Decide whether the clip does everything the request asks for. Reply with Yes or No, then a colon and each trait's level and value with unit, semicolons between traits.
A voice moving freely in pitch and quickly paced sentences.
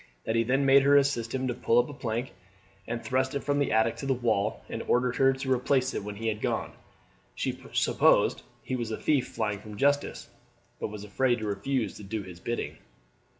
No: average, 3.5 semitones; fast, 220 wpm